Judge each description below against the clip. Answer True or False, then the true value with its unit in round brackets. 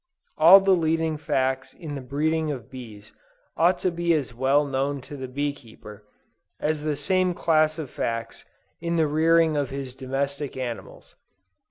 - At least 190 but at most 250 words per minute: False (165 wpm)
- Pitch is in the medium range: True (145 Hz)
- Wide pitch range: False (3.5 semitones)